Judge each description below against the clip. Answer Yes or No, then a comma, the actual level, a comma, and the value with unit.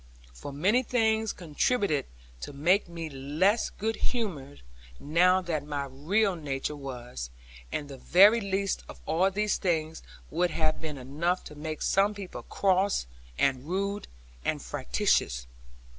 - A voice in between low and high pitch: Yes, medium, 165 Hz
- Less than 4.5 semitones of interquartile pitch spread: No, wide, 5.6 semitones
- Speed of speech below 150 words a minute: Yes, average, 140 wpm